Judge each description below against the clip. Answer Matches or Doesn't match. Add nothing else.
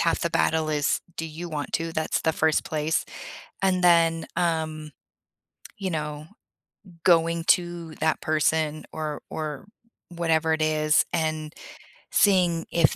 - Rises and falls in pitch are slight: Matches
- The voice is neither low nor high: Matches